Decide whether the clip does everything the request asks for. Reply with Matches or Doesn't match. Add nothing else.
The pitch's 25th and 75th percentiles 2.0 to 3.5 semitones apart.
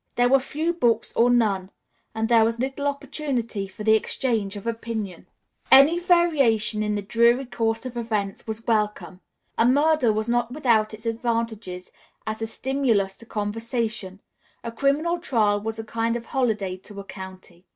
Matches